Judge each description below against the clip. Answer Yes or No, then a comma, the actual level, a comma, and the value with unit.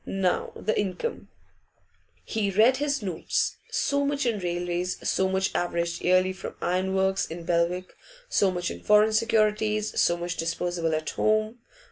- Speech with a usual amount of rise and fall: Yes, average, 3.5 semitones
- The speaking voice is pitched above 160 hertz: Yes, high, 190 Hz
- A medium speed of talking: Yes, average, 150 wpm